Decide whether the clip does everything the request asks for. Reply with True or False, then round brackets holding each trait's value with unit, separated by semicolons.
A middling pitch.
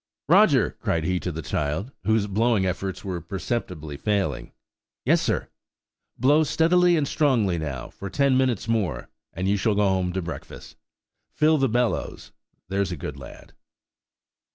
False (100 Hz)